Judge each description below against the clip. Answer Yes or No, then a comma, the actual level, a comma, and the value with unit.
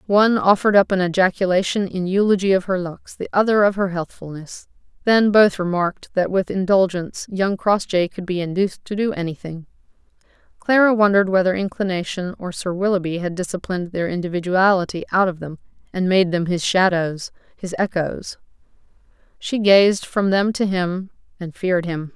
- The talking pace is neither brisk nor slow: Yes, average, 160 wpm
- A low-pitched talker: No, medium, 185 Hz